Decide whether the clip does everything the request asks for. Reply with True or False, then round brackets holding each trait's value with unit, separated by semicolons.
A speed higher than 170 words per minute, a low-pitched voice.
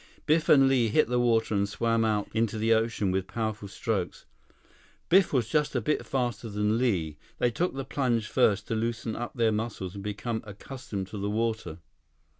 True (190 wpm; 115 Hz)